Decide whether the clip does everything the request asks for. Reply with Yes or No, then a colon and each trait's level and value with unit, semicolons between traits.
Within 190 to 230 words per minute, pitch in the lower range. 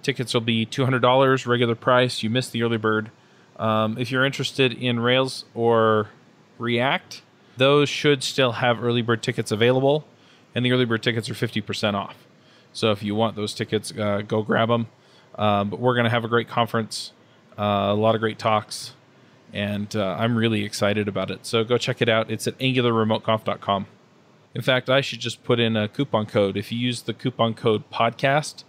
Yes: average, 200 wpm; low, 115 Hz